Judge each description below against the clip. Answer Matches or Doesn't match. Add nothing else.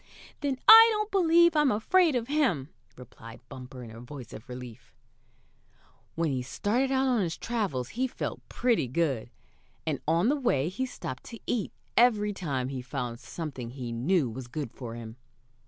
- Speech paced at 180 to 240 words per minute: Doesn't match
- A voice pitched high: Doesn't match